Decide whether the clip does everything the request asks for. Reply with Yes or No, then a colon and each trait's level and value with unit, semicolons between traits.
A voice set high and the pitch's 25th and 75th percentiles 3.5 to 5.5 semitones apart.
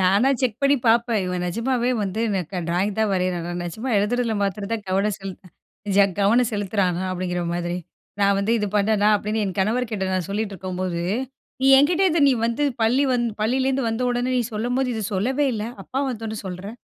Yes: high, 210 Hz; average, 4.2 semitones